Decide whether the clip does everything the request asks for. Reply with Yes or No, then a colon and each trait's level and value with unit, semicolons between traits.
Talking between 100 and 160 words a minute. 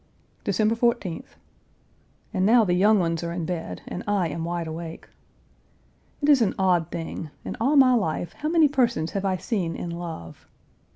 No: average, 175 wpm